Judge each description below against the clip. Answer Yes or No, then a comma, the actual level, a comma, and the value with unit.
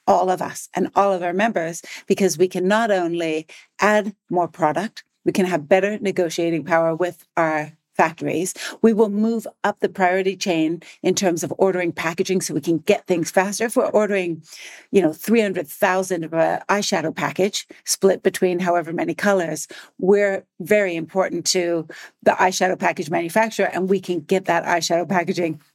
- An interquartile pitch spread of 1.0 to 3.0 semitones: Yes, average, 2.7 semitones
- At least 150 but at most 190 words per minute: Yes, average, 170 wpm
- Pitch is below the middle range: No, medium, 185 Hz